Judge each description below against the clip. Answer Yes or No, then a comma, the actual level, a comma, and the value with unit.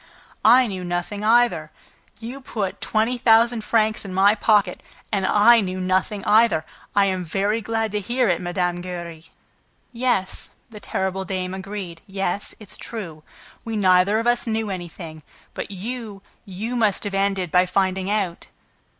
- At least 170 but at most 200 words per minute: No, average, 155 wpm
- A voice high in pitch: Yes, high, 200 Hz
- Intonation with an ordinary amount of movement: Yes, average, 3.4 semitones